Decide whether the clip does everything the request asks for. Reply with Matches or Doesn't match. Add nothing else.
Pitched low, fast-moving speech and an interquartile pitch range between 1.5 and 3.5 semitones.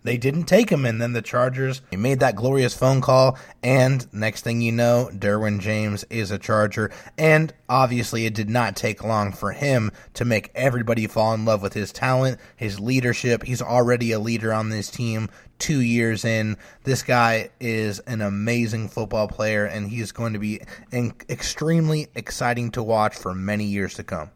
Doesn't match